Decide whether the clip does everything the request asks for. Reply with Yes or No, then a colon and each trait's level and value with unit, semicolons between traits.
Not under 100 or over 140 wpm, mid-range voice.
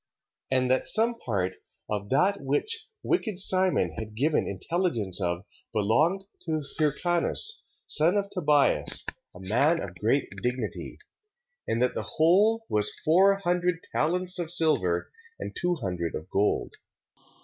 Yes: slow, 135 wpm; medium, 155 Hz